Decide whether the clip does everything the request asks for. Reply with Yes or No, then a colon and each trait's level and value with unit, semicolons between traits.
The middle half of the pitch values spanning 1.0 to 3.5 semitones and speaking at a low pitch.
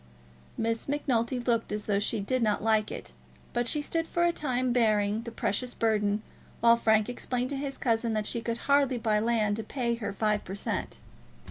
No: average, 2.9 semitones; high, 230 Hz